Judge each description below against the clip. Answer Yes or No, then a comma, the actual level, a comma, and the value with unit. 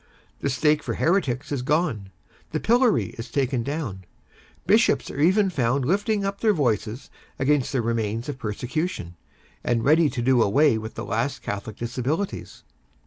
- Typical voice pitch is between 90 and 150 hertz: Yes, low, 135 Hz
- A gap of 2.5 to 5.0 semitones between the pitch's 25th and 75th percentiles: No, wide, 5.4 semitones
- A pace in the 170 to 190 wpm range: No, average, 155 wpm